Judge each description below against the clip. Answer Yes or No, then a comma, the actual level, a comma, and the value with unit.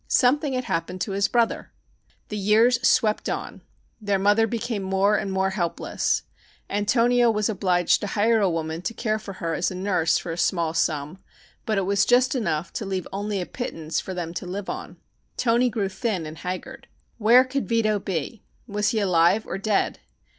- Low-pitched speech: No, high, 200 Hz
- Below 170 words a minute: No, average, 185 wpm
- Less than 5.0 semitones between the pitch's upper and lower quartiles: Yes, average, 3.9 semitones